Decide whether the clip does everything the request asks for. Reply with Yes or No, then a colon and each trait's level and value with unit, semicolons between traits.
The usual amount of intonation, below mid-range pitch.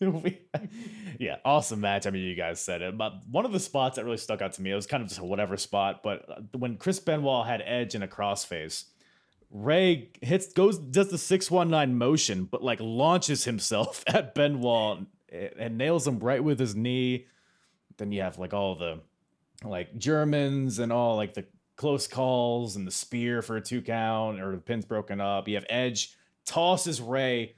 No: wide, 6.1 semitones; low, 120 Hz